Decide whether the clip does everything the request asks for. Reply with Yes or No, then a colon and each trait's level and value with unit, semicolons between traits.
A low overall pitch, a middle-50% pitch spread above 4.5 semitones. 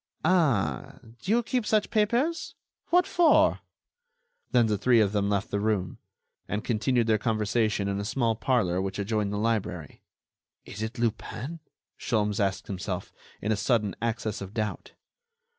No: low, 110 Hz; average, 3.6 semitones